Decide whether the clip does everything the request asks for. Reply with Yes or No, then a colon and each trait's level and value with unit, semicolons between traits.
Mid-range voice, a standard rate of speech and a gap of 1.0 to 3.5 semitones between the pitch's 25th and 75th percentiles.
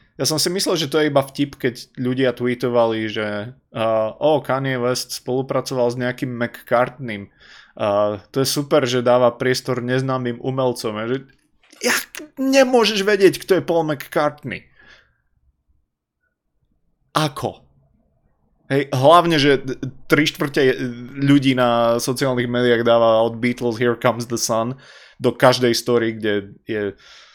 No: low, 125 Hz; average, 130 wpm; average, 2.9 semitones